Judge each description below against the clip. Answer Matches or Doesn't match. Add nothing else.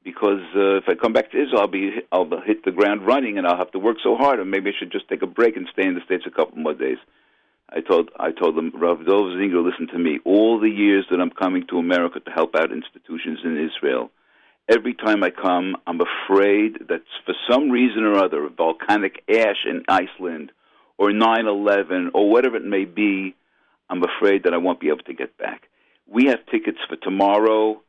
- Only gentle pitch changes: Matches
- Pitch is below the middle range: Matches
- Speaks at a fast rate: Matches